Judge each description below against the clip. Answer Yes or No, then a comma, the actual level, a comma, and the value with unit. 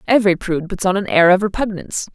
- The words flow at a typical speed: No, fast, 225 wpm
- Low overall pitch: No, high, 190 Hz